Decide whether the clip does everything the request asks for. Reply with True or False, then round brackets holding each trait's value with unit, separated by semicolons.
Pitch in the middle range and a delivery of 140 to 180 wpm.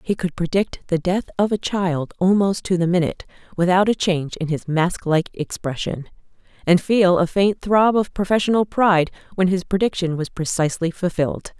True (180 Hz; 175 wpm)